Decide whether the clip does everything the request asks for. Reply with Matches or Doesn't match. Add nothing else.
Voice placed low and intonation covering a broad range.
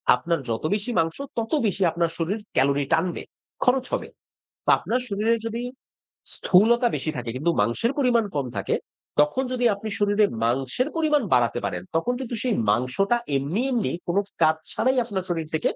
Doesn't match